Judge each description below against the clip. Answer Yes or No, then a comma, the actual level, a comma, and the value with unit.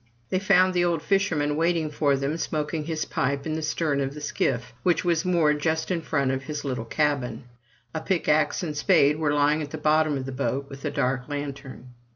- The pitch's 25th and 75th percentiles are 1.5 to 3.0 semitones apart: Yes, narrow, 2.6 semitones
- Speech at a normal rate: No, fast, 210 wpm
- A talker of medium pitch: Yes, medium, 150 Hz